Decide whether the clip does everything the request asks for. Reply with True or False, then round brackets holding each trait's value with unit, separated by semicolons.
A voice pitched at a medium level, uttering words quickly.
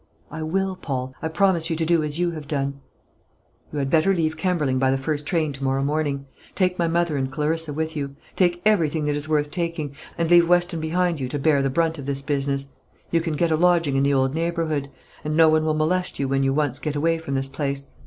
True (155 Hz; 240 wpm)